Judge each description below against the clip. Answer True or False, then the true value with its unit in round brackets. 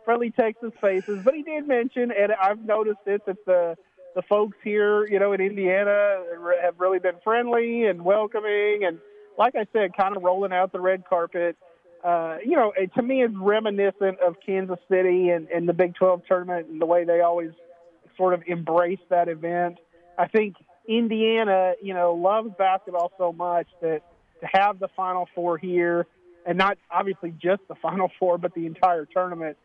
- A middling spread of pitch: True (3.0 semitones)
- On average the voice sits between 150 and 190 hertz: True (185 Hz)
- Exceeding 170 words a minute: True (185 wpm)